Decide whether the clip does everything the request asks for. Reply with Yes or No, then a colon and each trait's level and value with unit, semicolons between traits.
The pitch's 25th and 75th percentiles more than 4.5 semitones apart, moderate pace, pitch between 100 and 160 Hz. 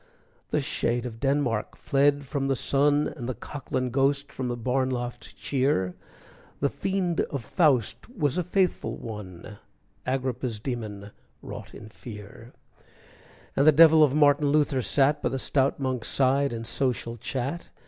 No: average, 3.1 semitones; average, 150 wpm; low, 135 Hz